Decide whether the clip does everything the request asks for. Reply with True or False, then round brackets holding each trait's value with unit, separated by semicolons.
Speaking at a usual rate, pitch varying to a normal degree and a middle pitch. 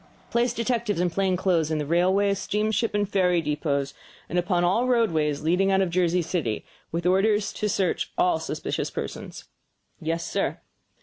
True (165 wpm; 3.8 semitones; 180 Hz)